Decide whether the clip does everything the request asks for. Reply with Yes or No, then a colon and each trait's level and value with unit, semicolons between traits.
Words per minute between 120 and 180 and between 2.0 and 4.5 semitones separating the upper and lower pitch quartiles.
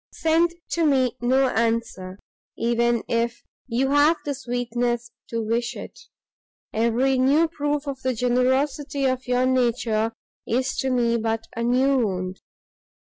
Yes: slow, 135 wpm; narrow, 2.6 semitones